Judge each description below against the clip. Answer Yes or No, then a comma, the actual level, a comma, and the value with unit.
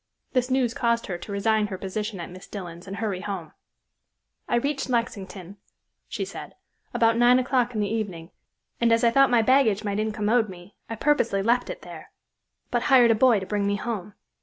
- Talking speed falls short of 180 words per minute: No, average, 195 wpm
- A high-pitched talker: Yes, high, 220 Hz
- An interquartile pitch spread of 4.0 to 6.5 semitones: No, average, 3.3 semitones